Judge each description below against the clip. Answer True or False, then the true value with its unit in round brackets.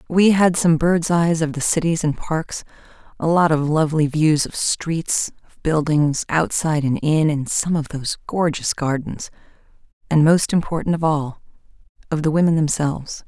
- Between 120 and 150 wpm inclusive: False (165 wpm)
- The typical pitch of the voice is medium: True (160 Hz)